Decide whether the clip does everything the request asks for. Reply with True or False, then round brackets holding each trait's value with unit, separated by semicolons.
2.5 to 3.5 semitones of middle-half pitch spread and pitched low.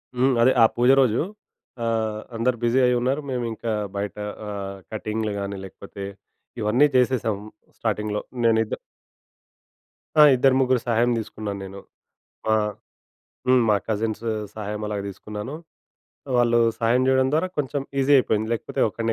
True (2.9 semitones; 115 Hz)